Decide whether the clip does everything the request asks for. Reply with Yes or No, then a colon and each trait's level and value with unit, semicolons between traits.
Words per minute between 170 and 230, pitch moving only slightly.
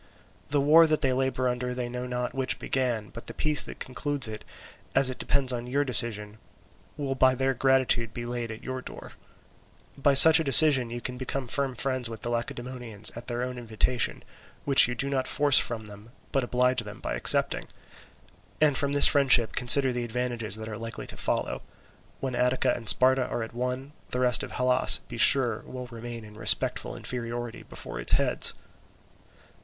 Yes: average, 190 wpm; narrow, 2.1 semitones